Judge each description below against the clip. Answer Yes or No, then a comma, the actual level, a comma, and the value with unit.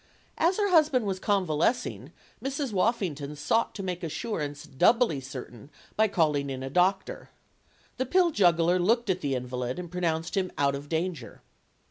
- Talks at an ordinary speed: Yes, average, 155 wpm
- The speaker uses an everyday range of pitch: No, wide, 7.6 semitones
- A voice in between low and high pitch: Yes, medium, 180 Hz